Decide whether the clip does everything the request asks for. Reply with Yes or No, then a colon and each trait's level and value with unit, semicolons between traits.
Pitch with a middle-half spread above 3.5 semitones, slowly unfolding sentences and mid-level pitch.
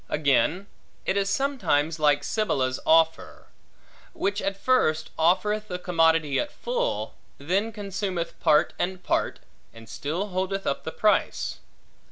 Yes: average, 4.7 semitones; slow, 130 wpm; medium, 180 Hz